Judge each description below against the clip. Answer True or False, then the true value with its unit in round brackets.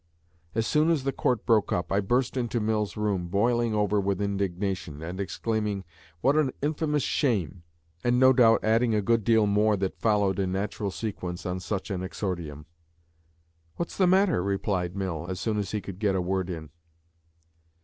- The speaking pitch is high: False (105 Hz)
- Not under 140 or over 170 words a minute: False (180 wpm)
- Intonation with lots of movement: False (3.8 semitones)